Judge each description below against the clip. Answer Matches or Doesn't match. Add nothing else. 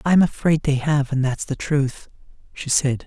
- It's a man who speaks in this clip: Matches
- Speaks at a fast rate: Matches